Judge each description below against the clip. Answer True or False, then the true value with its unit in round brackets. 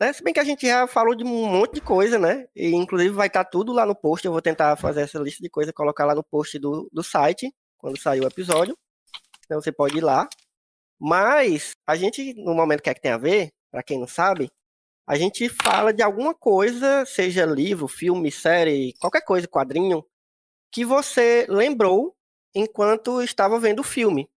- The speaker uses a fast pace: True (200 wpm)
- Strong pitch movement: True (7.7 semitones)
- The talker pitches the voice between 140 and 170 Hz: False (185 Hz)